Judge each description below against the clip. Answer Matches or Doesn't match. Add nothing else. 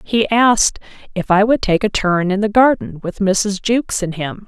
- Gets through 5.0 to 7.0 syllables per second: Doesn't match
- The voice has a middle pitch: Doesn't match